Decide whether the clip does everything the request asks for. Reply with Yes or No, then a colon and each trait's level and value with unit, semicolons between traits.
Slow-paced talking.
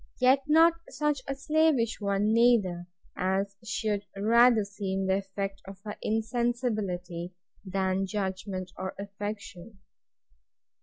Yes: slow, 110 wpm